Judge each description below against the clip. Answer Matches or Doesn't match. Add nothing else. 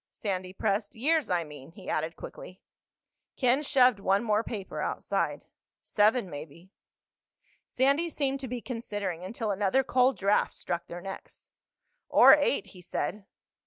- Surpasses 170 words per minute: Doesn't match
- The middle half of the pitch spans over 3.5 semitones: Matches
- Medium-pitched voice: Doesn't match